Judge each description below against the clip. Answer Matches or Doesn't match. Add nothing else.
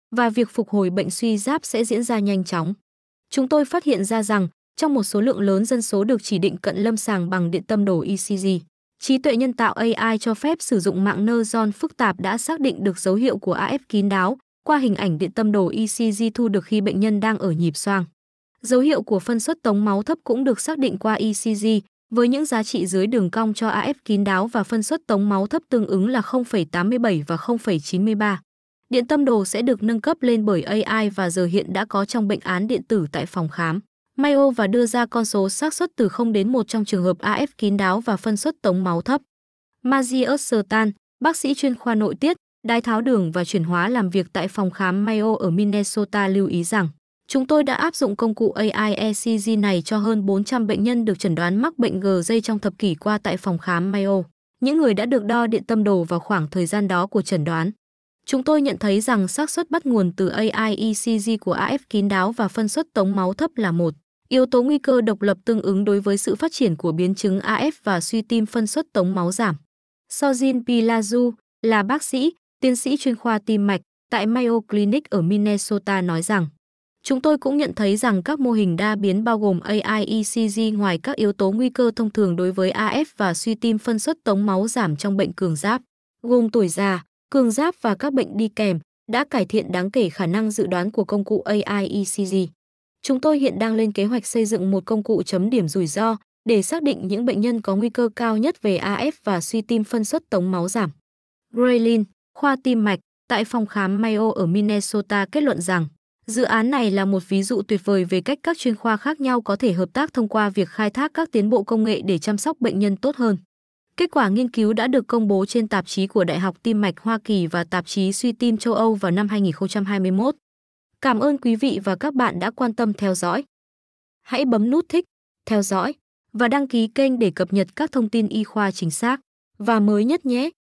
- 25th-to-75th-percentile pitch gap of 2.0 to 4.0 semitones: Matches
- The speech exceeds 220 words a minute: Matches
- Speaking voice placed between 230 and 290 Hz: Doesn't match